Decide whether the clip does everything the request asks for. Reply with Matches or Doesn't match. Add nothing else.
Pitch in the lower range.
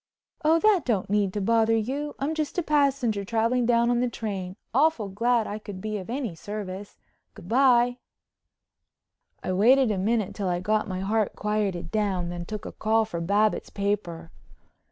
Doesn't match